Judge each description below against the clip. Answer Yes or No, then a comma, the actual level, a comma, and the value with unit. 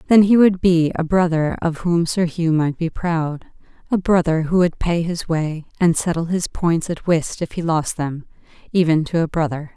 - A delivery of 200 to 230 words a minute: Yes, fast, 205 wpm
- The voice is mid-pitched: Yes, medium, 165 Hz